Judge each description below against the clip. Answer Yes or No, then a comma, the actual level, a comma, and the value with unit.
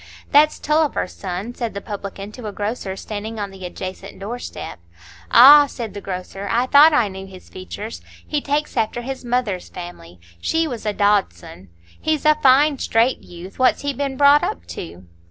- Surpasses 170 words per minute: Yes, average, 180 wpm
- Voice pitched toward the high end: Yes, high, 220 Hz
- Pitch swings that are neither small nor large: No, wide, 5.9 semitones